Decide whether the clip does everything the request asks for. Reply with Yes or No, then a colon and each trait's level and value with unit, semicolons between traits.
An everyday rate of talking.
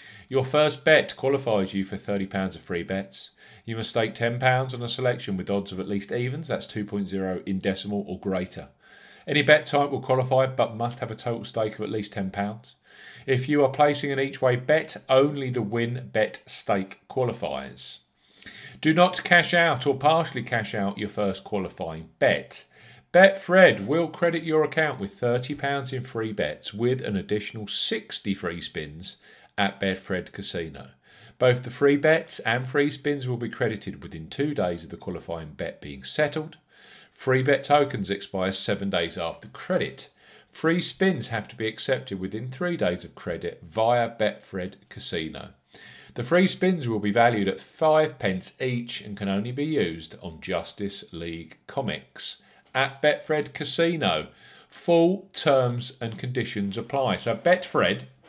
Yes: average, 165 wpm